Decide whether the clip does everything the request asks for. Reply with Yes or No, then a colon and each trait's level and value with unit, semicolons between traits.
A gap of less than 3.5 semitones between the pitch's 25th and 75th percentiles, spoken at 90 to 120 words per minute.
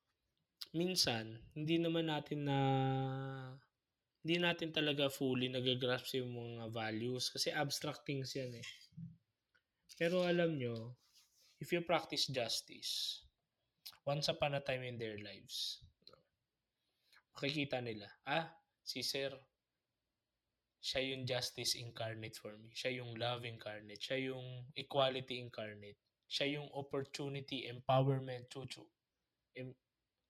Yes: average, 2.9 semitones; average, 115 wpm